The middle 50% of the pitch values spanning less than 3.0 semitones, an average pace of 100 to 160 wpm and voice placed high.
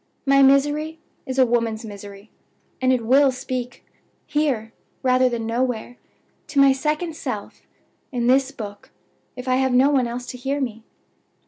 Yes: narrow, 2.6 semitones; average, 155 wpm; very high, 255 Hz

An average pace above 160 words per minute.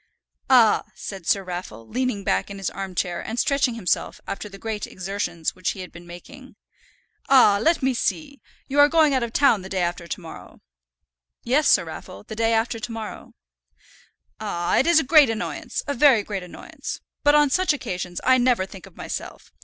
Yes: average, 190 wpm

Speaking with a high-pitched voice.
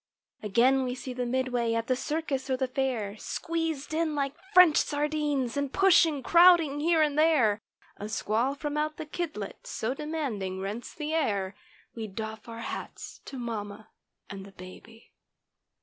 Yes: very high, 260 Hz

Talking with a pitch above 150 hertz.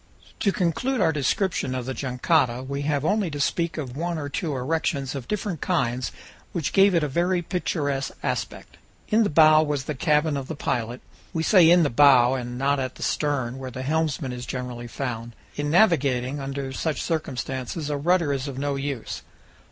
No: medium, 145 Hz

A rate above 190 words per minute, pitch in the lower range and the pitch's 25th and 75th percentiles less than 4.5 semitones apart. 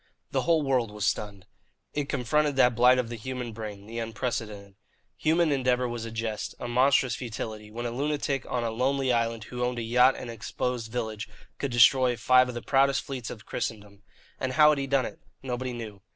Yes: fast, 205 wpm; low, 120 Hz; narrow, 2.6 semitones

